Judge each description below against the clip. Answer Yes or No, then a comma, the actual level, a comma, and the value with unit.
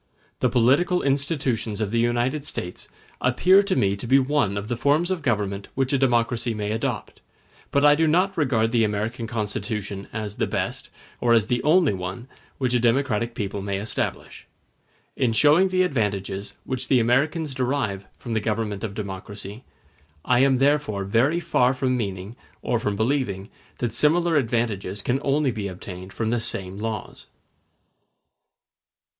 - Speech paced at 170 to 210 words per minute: No, average, 160 wpm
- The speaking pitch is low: Yes, low, 120 Hz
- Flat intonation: No, average, 4.9 semitones